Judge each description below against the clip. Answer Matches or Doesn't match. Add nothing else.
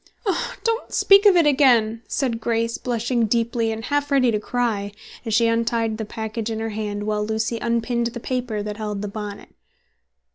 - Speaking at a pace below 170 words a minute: Doesn't match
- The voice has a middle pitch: Doesn't match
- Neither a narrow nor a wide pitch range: Doesn't match